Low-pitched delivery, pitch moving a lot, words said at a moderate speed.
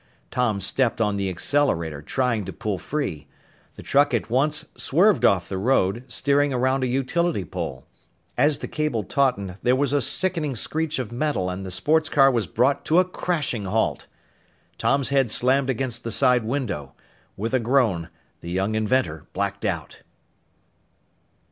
Yes: low, 125 Hz; wide, 5.9 semitones; average, 160 wpm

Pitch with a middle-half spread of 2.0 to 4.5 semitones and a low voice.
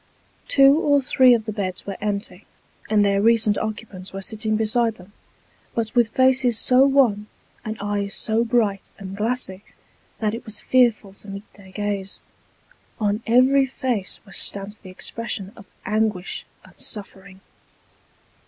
No: average, 3.0 semitones; high, 215 Hz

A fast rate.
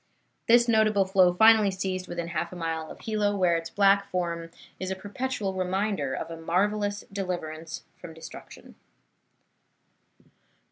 No: average, 140 wpm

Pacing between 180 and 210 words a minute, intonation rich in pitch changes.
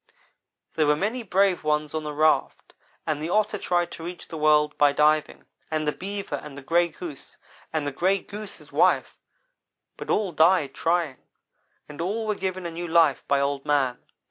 No: average, 190 wpm; average, 3.5 semitones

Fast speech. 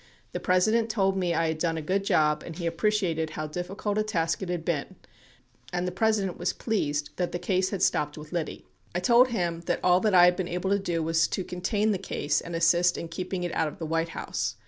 Yes: fast, 245 wpm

